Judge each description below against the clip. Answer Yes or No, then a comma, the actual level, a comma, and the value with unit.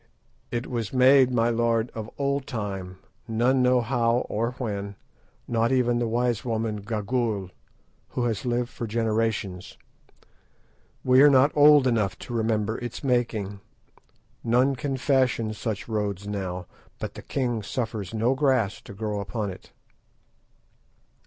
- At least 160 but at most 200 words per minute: No, average, 140 wpm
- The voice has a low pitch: Yes, low, 115 Hz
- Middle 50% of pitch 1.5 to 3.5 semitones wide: Yes, average, 3.1 semitones